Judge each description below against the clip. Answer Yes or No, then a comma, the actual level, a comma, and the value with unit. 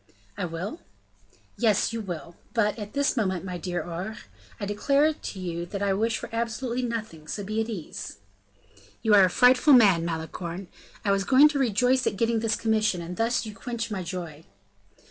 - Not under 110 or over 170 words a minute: No, average, 185 wpm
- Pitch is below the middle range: No, high, 210 Hz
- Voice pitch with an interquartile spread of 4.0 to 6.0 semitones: Yes, average, 4.4 semitones